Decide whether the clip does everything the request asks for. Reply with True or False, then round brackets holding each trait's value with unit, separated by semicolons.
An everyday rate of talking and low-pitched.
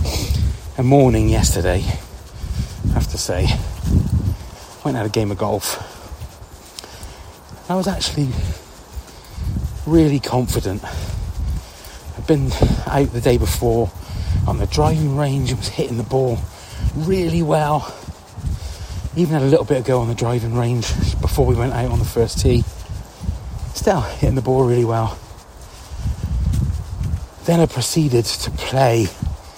False (130 wpm; 110 Hz)